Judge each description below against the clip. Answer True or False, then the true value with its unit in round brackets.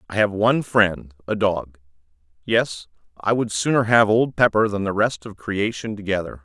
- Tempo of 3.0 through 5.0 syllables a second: True (4.8 syllables/s)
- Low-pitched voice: True (105 Hz)